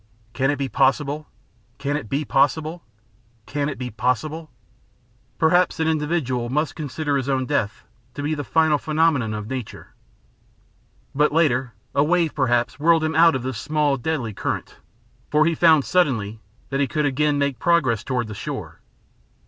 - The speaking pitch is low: No, medium, 145 Hz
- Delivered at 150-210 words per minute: Yes, average, 165 wpm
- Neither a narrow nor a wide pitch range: Yes, average, 3.3 semitones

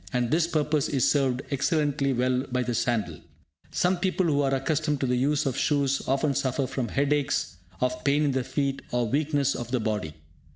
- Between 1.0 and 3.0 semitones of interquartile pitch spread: Yes, average, 2.7 semitones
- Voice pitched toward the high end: No, medium, 140 Hz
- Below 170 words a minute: No, average, 195 wpm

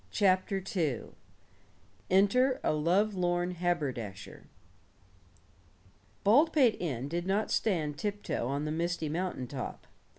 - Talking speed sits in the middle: No, slow, 100 wpm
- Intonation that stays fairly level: No, average, 5.0 semitones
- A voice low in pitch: No, medium, 175 Hz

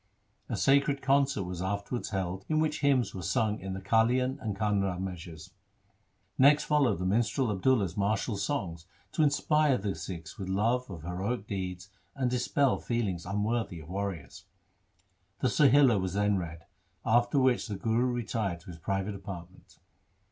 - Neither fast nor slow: Yes, average, 160 wpm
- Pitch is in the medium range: No, low, 105 Hz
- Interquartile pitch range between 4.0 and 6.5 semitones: Yes, average, 5.1 semitones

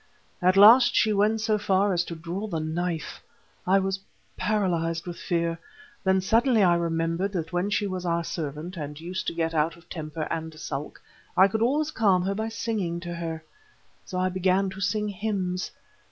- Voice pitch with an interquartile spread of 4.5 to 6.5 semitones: No, average, 3.3 semitones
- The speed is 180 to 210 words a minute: Yes, average, 185 wpm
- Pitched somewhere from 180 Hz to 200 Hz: Yes, medium, 185 Hz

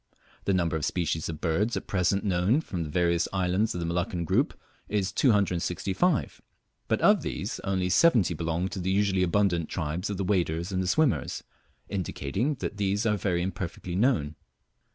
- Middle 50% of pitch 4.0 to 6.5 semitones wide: No, average, 2.9 semitones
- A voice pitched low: Yes, very low, 95 Hz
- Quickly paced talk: No, average, 170 wpm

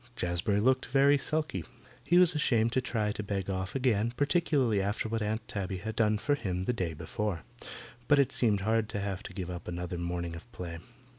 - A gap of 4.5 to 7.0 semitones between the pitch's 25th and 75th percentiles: Yes, average, 5.2 semitones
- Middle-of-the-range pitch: No, low, 105 Hz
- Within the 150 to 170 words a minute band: No, fast, 205 wpm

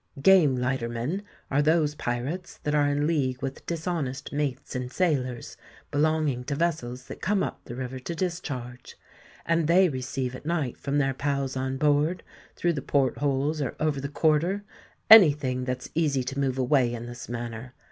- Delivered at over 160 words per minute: Yes, average, 175 wpm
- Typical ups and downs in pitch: Yes, average, 3.6 semitones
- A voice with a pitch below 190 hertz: Yes, medium, 140 Hz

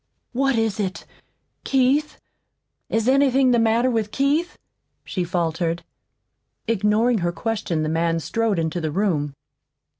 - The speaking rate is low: Yes, slow, 125 wpm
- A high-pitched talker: Yes, high, 215 Hz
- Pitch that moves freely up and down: Yes, wide, 6.5 semitones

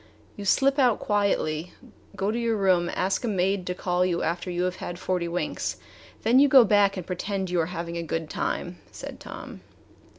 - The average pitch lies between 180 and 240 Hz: Yes, medium, 185 Hz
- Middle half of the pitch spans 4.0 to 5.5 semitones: No, average, 2.8 semitones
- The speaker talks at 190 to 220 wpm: Yes, average, 200 wpm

